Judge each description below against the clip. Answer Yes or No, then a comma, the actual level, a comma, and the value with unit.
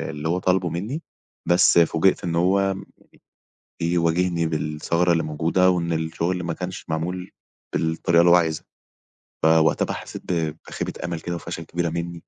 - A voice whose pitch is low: Yes, very low, 85 Hz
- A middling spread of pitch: No, narrow, 1.6 semitones